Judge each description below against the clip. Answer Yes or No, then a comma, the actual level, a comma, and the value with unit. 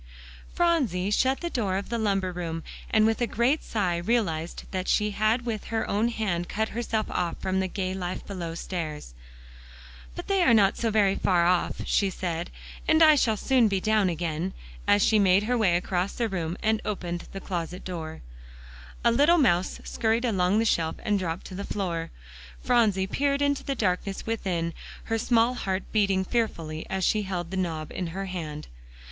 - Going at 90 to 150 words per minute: No, average, 190 wpm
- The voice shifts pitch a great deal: No, average, 4.2 semitones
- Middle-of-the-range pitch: No, high, 195 Hz